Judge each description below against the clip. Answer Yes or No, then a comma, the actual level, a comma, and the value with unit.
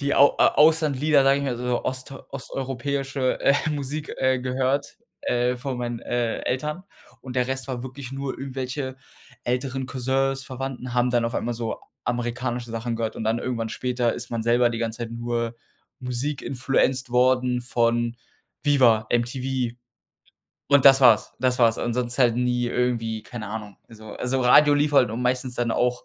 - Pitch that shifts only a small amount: Yes, narrow, 2.0 semitones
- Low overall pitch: Yes, low, 125 Hz